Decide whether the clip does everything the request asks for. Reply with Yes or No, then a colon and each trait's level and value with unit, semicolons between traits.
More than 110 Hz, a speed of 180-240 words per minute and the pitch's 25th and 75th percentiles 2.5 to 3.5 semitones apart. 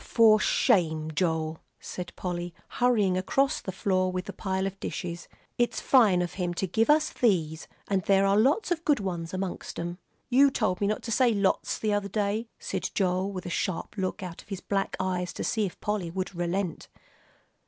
Yes: high, 190 Hz; average, 195 wpm; average, 3.2 semitones